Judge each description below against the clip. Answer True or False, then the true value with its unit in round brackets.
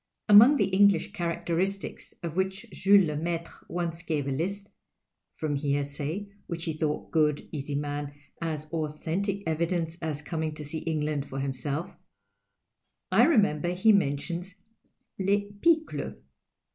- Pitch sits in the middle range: True (165 Hz)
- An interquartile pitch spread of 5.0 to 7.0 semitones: False (4.2 semitones)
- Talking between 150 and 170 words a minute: False (135 wpm)